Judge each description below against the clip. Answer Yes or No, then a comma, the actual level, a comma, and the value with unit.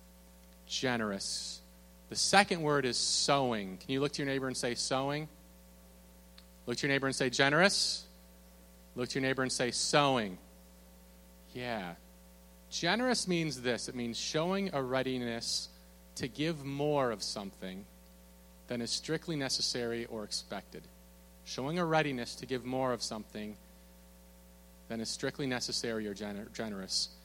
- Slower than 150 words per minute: Yes, average, 140 wpm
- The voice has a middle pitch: No, low, 115 Hz